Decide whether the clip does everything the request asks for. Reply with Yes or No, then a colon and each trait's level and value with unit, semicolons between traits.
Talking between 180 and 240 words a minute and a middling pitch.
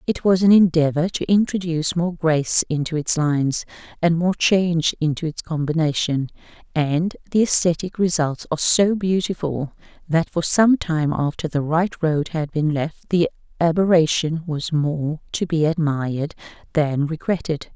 No: average, 150 wpm; medium, 160 Hz